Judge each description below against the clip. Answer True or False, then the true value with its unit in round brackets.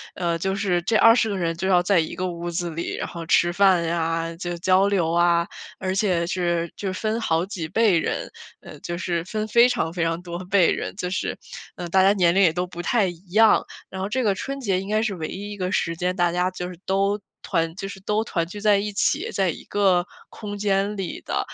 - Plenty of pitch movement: False (2.7 semitones)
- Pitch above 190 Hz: False (185 Hz)